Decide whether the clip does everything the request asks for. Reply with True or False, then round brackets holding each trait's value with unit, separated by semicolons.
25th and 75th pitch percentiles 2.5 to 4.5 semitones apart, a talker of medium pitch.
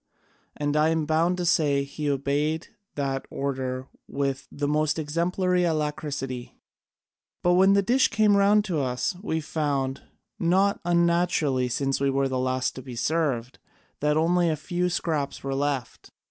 True (4.0 semitones; 150 Hz)